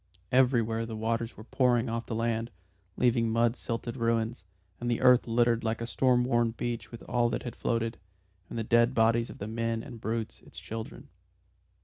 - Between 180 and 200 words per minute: Yes, average, 190 wpm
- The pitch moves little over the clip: Yes, narrow, 1.0 semitones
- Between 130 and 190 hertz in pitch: No, low, 115 Hz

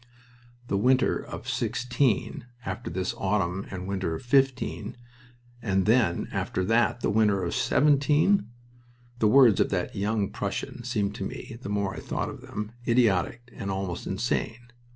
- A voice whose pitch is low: Yes, low, 105 Hz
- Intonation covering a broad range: No, average, 3.9 semitones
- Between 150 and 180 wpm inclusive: Yes, average, 155 wpm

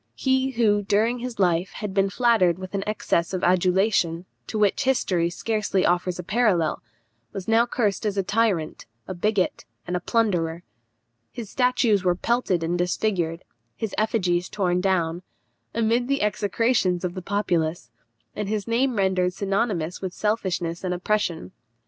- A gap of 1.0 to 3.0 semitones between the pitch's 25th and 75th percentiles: No, average, 3.8 semitones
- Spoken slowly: No, average, 155 wpm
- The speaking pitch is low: No, high, 195 Hz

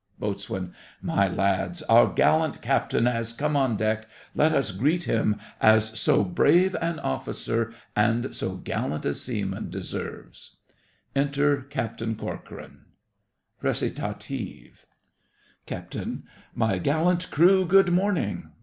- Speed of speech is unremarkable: No, slow, 115 wpm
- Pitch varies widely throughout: Yes, wide, 6.5 semitones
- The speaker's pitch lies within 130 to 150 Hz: No, low, 120 Hz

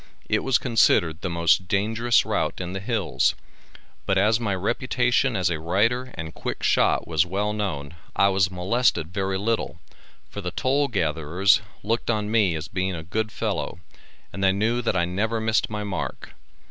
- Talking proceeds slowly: No, average, 175 wpm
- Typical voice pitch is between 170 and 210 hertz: No, low, 100 Hz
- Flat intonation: No, average, 4.0 semitones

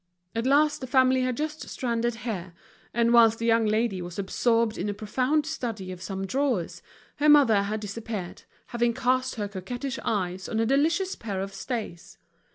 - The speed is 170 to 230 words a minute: Yes, average, 175 wpm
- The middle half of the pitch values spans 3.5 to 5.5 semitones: Yes, average, 4.3 semitones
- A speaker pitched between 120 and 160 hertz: No, high, 230 Hz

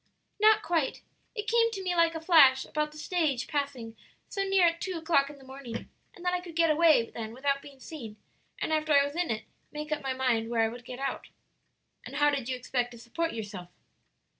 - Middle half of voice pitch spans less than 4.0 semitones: No, average, 5.1 semitones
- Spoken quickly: Yes, fast, 225 wpm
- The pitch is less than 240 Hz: No, very high, 290 Hz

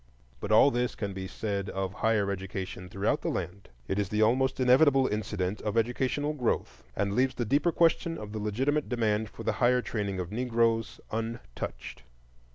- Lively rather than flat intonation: No, average, 4.0 semitones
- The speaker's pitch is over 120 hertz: No, low, 110 Hz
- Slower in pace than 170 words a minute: No, average, 175 wpm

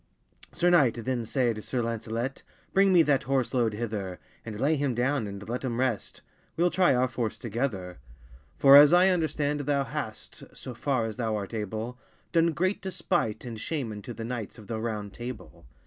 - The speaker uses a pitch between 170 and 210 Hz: No, low, 125 Hz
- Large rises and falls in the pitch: No, average, 4.5 semitones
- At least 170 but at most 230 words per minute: Yes, average, 185 wpm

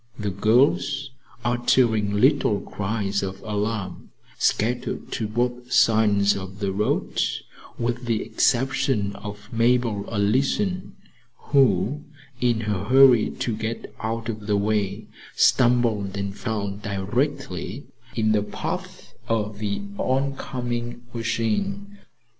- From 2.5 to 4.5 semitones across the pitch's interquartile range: Yes, average, 3.2 semitones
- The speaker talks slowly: Yes, slow, 110 wpm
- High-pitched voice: No, low, 110 Hz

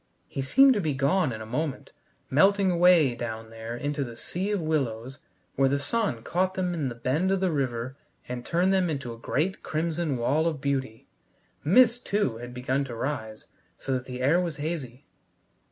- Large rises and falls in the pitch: Yes, wide, 5.9 semitones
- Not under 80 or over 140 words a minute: No, average, 190 wpm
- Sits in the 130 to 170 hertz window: Yes, medium, 140 Hz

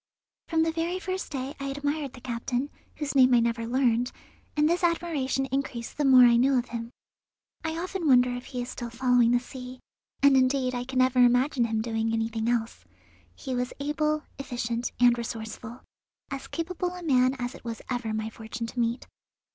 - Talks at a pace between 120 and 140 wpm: No, average, 190 wpm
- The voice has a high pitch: Yes, very high, 255 Hz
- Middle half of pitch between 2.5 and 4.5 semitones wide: Yes, average, 3.0 semitones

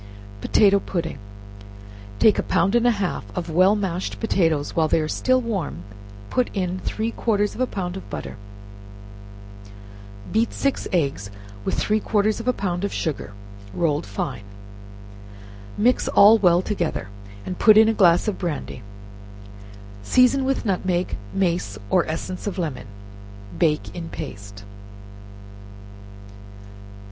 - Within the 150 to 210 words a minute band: No, slow, 135 wpm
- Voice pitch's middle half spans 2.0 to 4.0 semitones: No, average, 4.7 semitones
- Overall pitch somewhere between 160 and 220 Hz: Yes, medium, 185 Hz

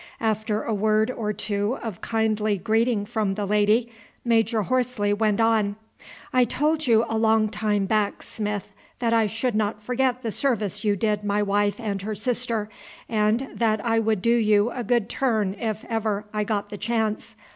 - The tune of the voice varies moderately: No, narrow, 1.8 semitones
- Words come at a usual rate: Yes, average, 180 wpm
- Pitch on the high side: Yes, high, 220 Hz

